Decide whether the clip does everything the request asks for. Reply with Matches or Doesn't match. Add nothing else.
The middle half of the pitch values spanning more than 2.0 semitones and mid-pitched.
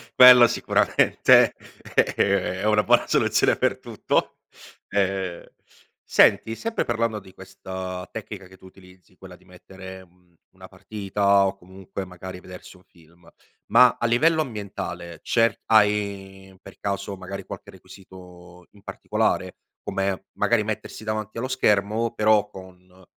Doesn't match